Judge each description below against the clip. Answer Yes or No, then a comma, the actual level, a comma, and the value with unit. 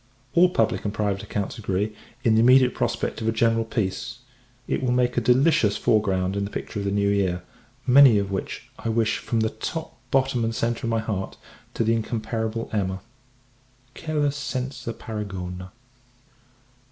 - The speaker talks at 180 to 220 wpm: No, average, 170 wpm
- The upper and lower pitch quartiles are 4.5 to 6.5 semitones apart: No, average, 3.4 semitones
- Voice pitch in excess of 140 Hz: No, low, 110 Hz